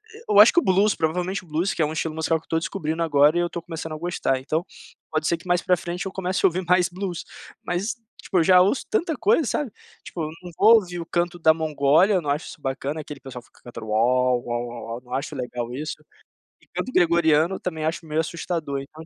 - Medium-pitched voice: Yes, medium, 165 Hz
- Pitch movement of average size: Yes, average, 3.5 semitones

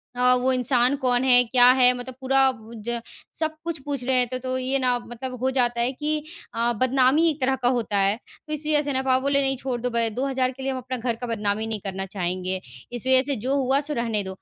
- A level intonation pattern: Yes, narrow, 2.0 semitones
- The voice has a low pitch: No, very high, 255 Hz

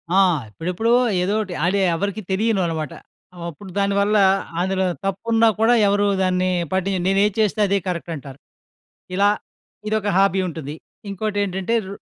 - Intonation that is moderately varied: No, narrow, 2.2 semitones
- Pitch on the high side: Yes, high, 195 Hz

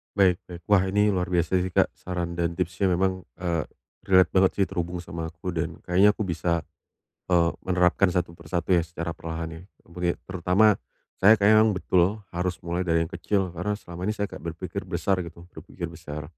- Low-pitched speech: Yes, very low, 90 Hz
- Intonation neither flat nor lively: No, narrow, 2.0 semitones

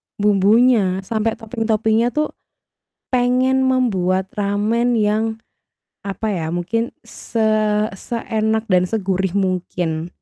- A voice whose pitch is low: No, high, 215 Hz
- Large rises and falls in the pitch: No, average, 3.4 semitones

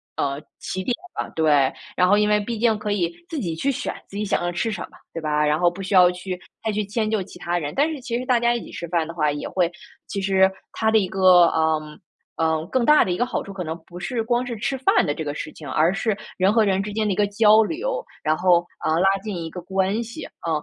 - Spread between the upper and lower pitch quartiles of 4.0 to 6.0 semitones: Yes, average, 4.5 semitones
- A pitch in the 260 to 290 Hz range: No, high, 190 Hz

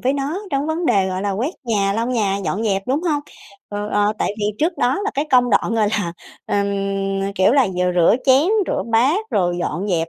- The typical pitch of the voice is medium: No, high, 220 Hz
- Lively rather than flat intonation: Yes, wide, 5.8 semitones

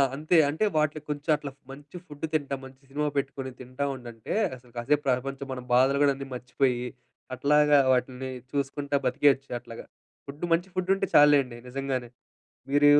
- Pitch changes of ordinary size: No, narrow, 2.3 semitones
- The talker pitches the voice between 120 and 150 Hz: Yes, medium, 140 Hz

